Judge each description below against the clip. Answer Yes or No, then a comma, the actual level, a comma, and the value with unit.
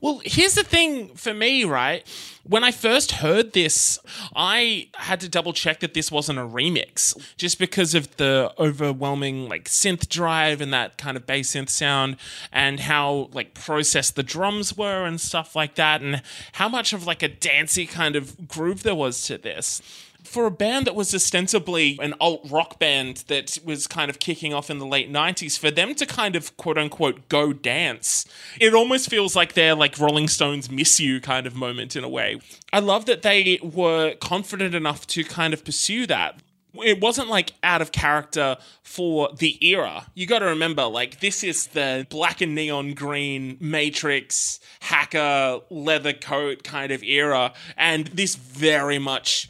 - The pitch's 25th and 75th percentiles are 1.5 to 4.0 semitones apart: No, average, 4.5 semitones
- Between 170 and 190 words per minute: Yes, average, 185 wpm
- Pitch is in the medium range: Yes, medium, 155 Hz